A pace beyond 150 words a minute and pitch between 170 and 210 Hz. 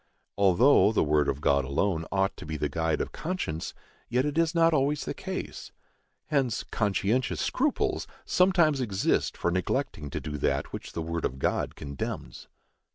No: average, 165 wpm; low, 100 Hz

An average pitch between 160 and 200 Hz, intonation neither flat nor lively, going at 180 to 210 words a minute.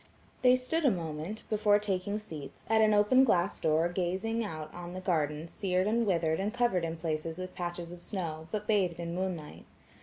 Yes: medium, 185 Hz; average, 4.1 semitones; average, 190 wpm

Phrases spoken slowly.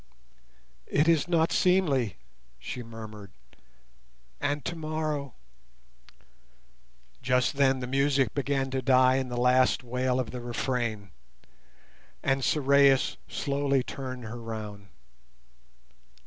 Yes: slow, 105 wpm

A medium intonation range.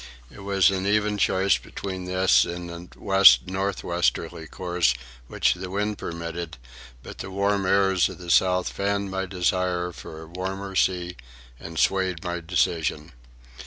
No: narrow, 2.0 semitones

